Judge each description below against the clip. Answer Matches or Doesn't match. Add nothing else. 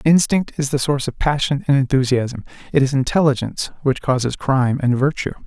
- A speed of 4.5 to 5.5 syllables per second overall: Doesn't match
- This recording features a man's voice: Matches